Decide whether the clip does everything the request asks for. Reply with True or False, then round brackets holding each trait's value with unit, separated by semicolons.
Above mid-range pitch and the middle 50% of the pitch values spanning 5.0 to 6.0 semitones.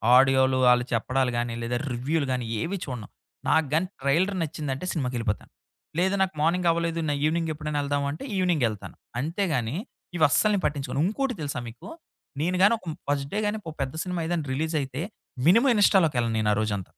False (150 Hz; 5.3 semitones)